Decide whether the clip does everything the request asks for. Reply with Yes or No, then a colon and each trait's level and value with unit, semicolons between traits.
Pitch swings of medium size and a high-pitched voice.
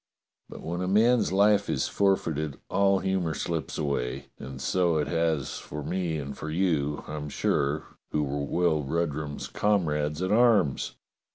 No: average, 4.4 semitones; very low, 80 Hz